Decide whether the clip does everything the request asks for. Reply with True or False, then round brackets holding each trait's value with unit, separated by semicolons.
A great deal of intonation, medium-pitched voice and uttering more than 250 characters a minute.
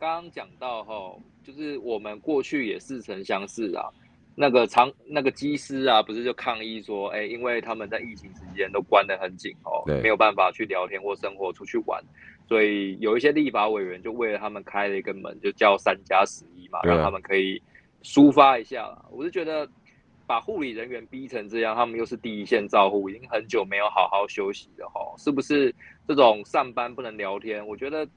False (5.8 semitones; 115 Hz; 300 characters per minute)